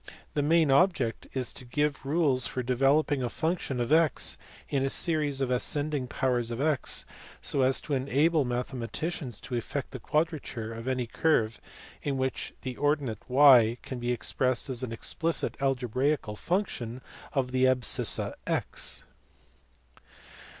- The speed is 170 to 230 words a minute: No, average, 150 wpm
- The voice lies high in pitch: No, low, 130 Hz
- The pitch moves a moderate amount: Yes, average, 3.2 semitones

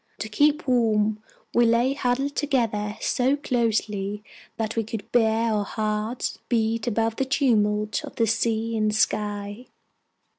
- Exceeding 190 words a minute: No, slow, 135 wpm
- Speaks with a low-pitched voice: No, high, 225 Hz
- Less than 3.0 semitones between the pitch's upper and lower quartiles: Yes, narrow, 2.5 semitones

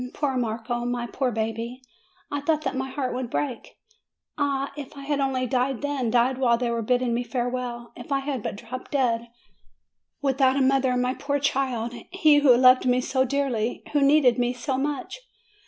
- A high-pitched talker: Yes, very high, 255 Hz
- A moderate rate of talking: Yes, average, 195 wpm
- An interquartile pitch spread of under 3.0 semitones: Yes, narrow, 2.4 semitones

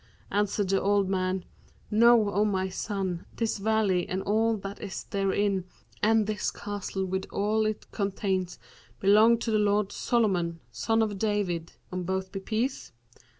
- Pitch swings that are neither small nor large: No, narrow, 2.2 semitones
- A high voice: Yes, high, 200 Hz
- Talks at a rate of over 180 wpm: No, average, 150 wpm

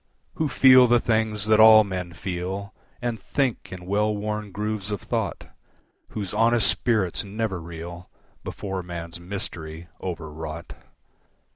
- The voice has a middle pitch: No, low, 100 Hz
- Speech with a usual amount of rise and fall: Yes, average, 3.8 semitones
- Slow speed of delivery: Yes, slow, 130 wpm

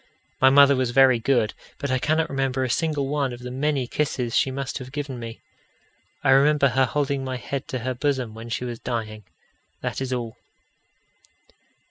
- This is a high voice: No, low, 130 Hz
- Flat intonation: Yes, narrow, 2.2 semitones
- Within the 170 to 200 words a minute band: Yes, average, 185 wpm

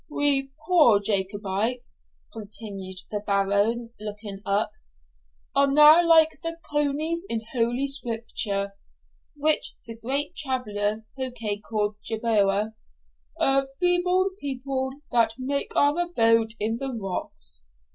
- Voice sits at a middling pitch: No, high, 230 Hz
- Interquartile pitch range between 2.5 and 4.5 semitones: No, average, 5.3 semitones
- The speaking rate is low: Yes, slow, 110 wpm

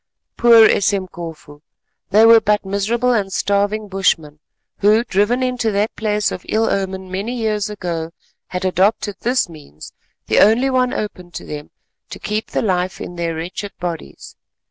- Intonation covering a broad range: No, average, 3.4 semitones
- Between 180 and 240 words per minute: No, average, 155 wpm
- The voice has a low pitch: No, high, 200 Hz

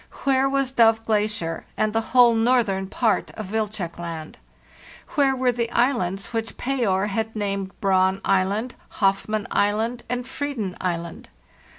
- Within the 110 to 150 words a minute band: Yes, average, 145 wpm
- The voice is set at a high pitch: Yes, high, 215 Hz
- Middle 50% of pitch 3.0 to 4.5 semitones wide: Yes, average, 3.8 semitones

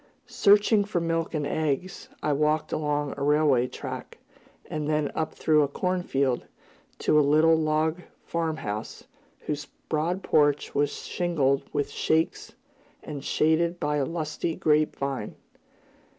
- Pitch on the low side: No, medium, 155 Hz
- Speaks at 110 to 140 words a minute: Yes, slow, 135 wpm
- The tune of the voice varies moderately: No, narrow, 2.1 semitones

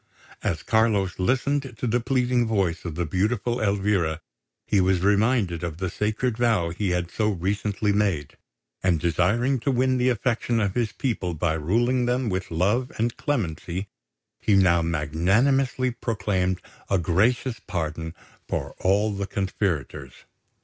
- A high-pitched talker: No, low, 100 Hz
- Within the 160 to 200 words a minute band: No, average, 145 wpm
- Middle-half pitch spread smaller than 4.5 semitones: No, average, 5.3 semitones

